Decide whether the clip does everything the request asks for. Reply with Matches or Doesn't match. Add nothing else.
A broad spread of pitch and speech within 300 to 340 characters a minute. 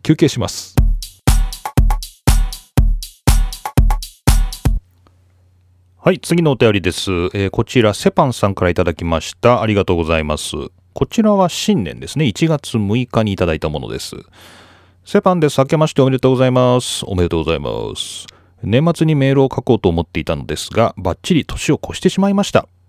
Matches